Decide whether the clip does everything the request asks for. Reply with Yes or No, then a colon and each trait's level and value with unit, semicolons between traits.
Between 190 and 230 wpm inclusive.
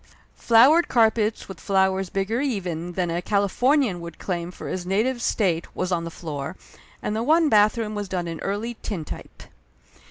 No: average, 170 wpm